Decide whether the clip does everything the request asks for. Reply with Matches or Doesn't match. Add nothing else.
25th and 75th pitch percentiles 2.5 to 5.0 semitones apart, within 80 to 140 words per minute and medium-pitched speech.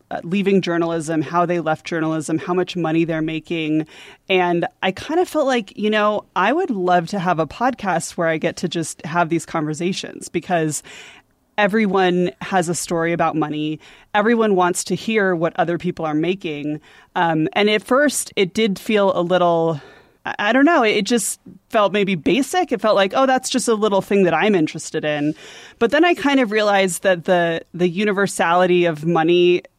Doesn't match